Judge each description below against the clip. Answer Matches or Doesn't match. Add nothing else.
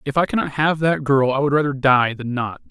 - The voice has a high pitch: Doesn't match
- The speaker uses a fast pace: Matches